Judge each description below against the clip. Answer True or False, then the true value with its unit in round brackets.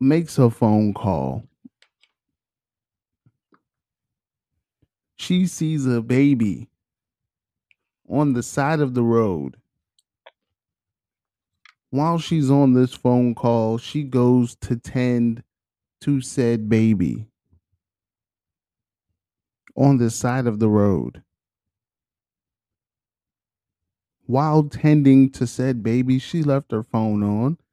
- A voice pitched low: True (115 Hz)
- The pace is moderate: False (95 wpm)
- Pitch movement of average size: True (4.7 semitones)